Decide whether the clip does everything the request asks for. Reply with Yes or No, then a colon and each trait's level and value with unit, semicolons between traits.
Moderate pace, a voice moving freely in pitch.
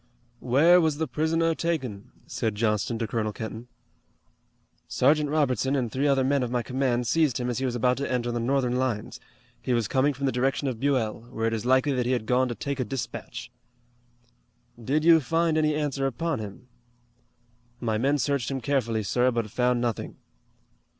No: average, 190 wpm; average, 3.2 semitones